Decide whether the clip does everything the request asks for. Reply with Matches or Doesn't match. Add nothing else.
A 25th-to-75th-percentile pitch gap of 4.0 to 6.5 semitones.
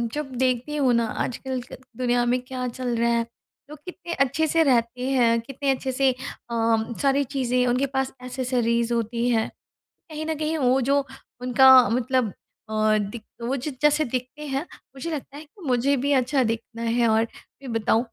Doesn't match